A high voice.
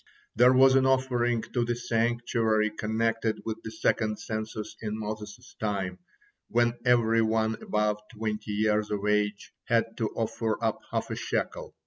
No: low, 110 Hz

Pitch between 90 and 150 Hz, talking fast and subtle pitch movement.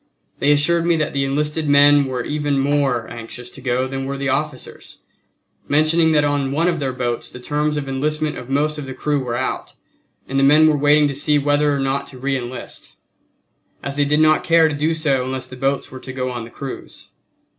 Yes: medium, 140 Hz; fast, 220 wpm; narrow, 2.2 semitones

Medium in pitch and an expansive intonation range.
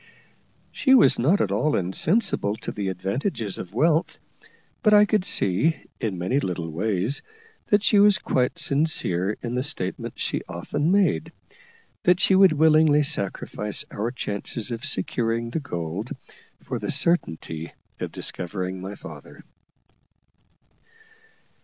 No: low, 120 Hz; wide, 9.0 semitones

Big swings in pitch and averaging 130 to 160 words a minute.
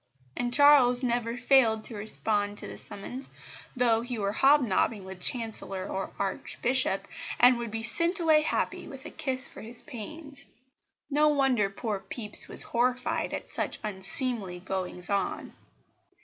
No: average, 4.3 semitones; average, 150 wpm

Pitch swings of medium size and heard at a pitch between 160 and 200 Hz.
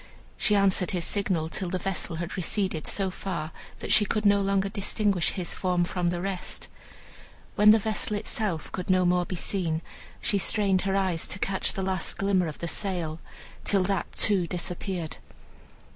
No: narrow, 2.2 semitones; high, 190 Hz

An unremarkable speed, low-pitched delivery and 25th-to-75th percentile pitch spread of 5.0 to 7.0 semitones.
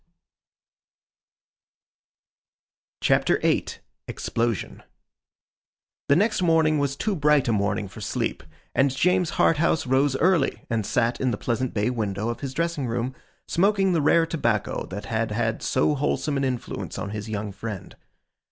Yes: average, 145 wpm; low, 130 Hz; wide, 5.6 semitones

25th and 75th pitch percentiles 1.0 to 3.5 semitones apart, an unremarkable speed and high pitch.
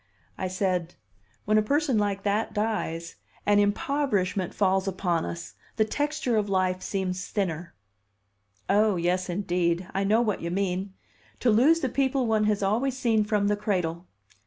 Yes: average, 3.1 semitones; average, 160 wpm; high, 200 Hz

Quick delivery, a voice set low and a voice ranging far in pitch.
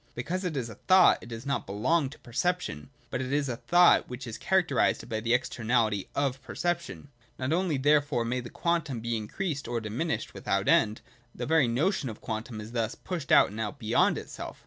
Yes: fast, 215 wpm; low, 130 Hz; wide, 5.7 semitones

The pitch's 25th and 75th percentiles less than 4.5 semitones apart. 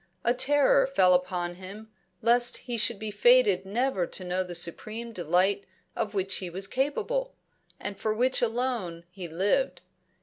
No: average, 5.2 semitones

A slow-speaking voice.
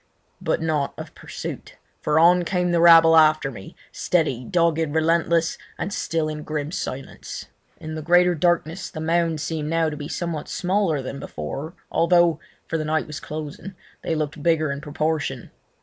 No: average, 160 wpm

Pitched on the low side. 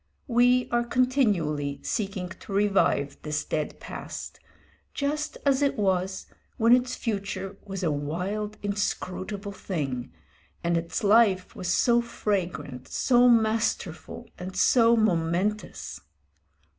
No: high, 200 Hz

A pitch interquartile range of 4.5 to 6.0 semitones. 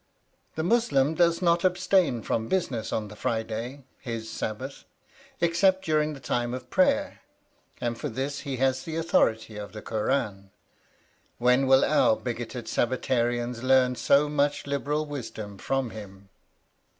Yes: average, 4.8 semitones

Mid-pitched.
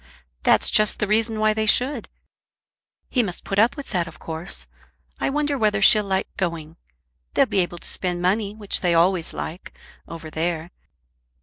No: high, 195 Hz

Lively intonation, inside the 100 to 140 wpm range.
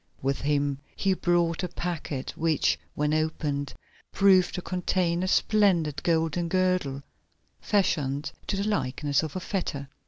No: average, 4.2 semitones; slow, 135 wpm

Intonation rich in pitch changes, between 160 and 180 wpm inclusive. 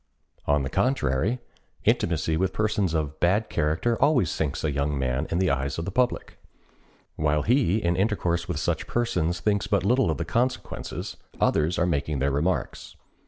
Yes: wide, 5.9 semitones; average, 170 wpm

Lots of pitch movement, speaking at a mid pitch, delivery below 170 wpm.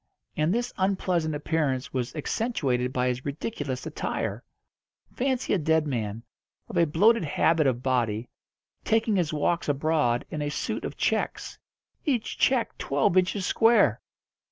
Yes: wide, 6.5 semitones; medium, 155 Hz; average, 140 wpm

